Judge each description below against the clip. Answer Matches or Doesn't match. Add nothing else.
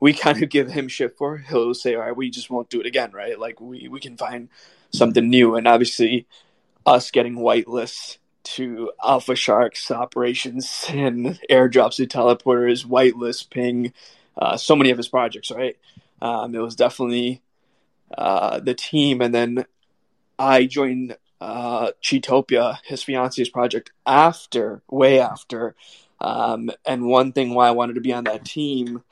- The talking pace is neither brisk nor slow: Matches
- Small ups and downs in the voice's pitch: Matches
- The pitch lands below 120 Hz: Doesn't match